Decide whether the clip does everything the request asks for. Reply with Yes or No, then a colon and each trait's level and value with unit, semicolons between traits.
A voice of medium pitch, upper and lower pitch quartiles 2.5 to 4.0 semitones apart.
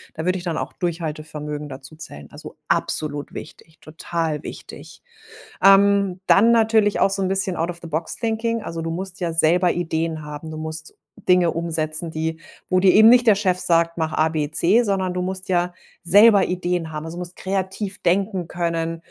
Yes: medium, 175 Hz; average, 3.1 semitones